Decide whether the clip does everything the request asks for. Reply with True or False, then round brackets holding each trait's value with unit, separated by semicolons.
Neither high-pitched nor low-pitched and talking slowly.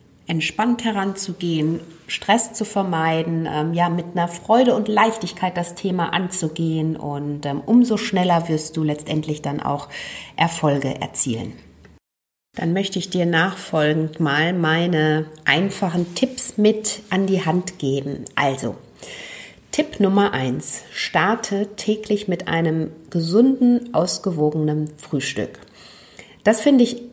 True (175 Hz; 120 wpm)